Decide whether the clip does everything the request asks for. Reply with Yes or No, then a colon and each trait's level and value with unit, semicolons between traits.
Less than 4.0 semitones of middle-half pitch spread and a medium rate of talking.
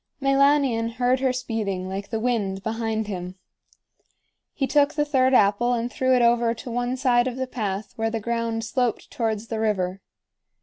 Yes: average, 2.8 semitones; average, 175 wpm